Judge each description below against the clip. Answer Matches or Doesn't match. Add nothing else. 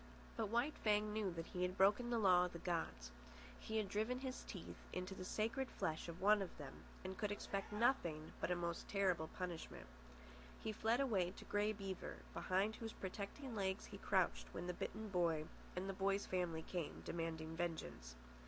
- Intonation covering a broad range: Doesn't match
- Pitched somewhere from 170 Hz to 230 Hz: Matches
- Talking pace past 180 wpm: Matches